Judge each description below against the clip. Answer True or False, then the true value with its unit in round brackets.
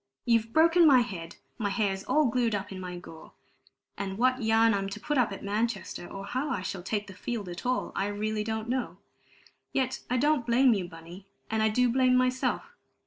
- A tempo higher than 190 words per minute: True (205 wpm)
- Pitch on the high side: True (220 Hz)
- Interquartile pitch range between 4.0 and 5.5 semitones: True (4.3 semitones)